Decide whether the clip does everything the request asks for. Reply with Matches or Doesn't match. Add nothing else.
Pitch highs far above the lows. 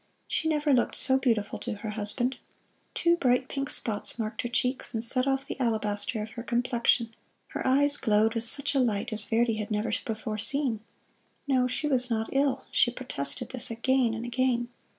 Doesn't match